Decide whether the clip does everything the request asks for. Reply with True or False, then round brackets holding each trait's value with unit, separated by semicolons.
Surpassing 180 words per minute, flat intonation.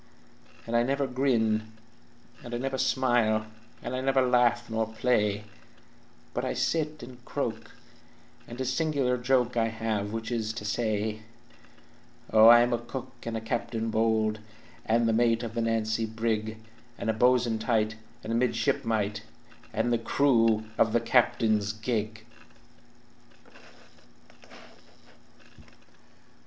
False (135 wpm; 1.9 semitones)